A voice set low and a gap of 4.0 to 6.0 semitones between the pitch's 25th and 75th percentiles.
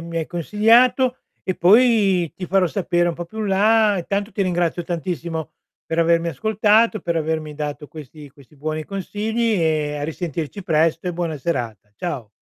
No: medium, 175 Hz; average, 4.5 semitones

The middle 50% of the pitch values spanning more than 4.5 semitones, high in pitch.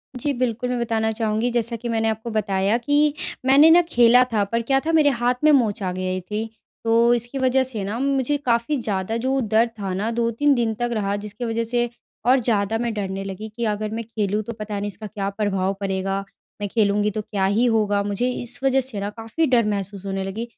No: average, 3.0 semitones; high, 225 Hz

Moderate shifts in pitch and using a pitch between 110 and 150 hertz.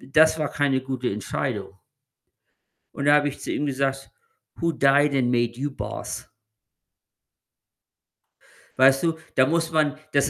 No: narrow, 2.2 semitones; medium, 140 Hz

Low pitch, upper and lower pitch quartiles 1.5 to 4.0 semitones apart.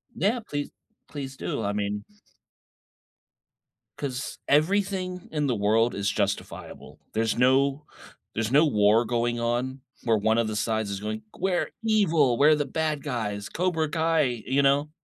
No: low, 130 Hz; wide, 5.6 semitones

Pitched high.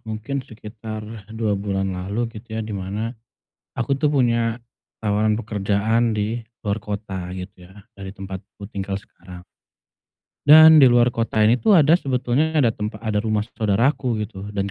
No: low, 110 Hz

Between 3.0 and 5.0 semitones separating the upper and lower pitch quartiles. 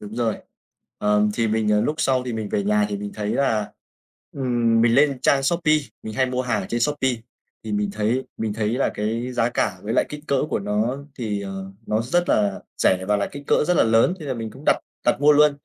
Yes: average, 4.0 semitones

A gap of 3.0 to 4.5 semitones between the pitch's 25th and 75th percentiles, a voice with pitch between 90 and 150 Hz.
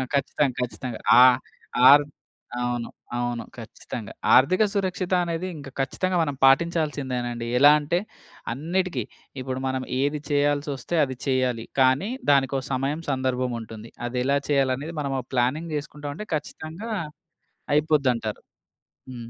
Yes: average, 3.3 semitones; low, 135 Hz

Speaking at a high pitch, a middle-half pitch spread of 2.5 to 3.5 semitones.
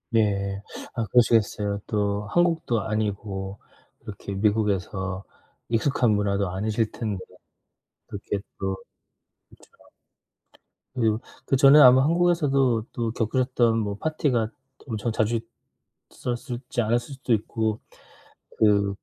No: low, 110 Hz; average, 3.2 semitones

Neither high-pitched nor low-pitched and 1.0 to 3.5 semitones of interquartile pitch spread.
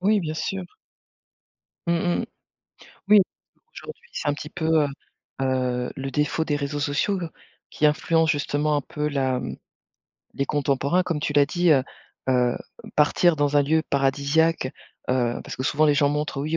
Yes: medium, 145 Hz; narrow, 2.5 semitones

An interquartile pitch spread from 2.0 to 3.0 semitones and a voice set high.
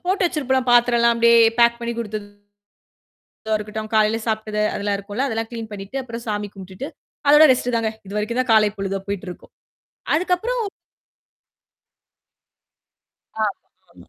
Yes: narrow, 2.6 semitones; high, 225 Hz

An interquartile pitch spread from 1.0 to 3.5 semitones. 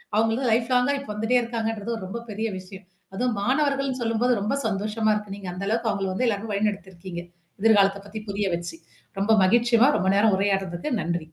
Yes: average, 3.1 semitones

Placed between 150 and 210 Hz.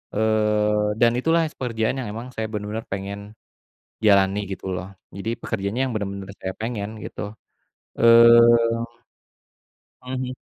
No: low, 110 Hz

